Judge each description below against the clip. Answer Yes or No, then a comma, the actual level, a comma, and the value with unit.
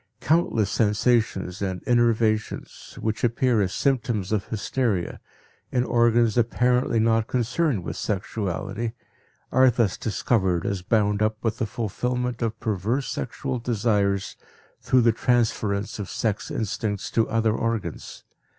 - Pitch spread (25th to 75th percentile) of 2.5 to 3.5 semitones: Yes, average, 2.8 semitones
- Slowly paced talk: Yes, slow, 125 wpm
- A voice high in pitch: No, low, 115 Hz